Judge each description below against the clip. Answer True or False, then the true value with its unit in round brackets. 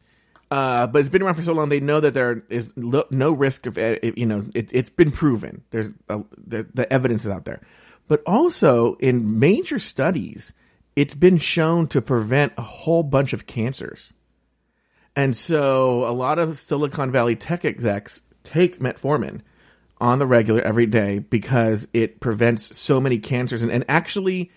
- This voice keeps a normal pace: True (175 wpm)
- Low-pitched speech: True (125 Hz)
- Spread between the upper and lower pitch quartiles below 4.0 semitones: False (4.3 semitones)